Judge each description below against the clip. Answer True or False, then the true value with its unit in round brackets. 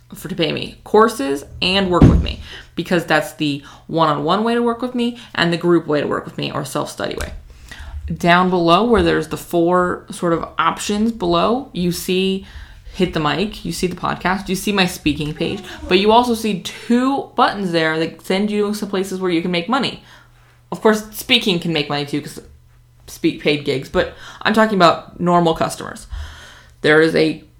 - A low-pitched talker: False (175 Hz)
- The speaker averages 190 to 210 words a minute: True (200 wpm)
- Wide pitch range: False (5.0 semitones)